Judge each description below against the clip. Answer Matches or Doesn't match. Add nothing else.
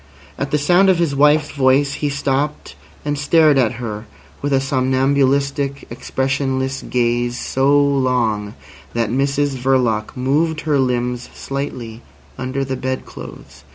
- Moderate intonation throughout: Doesn't match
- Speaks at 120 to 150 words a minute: Matches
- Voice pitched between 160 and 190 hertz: Doesn't match